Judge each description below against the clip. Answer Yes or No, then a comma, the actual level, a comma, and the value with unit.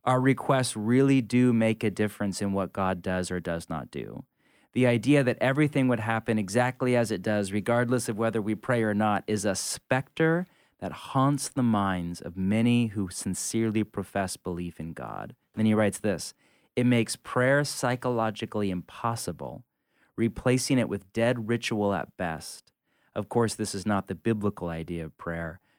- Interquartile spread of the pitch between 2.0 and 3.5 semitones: No, average, 4.2 semitones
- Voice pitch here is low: Yes, low, 110 Hz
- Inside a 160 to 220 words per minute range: Yes, average, 170 wpm